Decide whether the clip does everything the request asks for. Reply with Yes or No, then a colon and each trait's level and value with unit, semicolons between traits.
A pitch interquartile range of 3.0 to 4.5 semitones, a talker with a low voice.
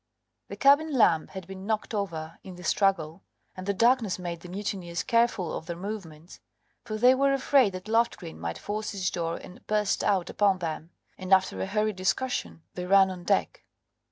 No: average, 3.6 semitones; high, 190 Hz